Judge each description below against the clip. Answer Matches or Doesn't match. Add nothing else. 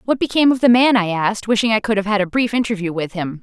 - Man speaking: Doesn't match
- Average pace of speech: Doesn't match